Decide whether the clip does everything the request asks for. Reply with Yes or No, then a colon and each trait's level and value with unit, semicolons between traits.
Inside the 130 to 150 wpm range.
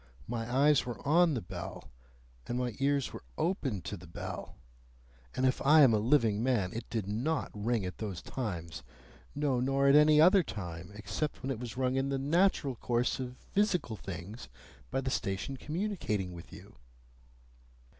No: average, 175 wpm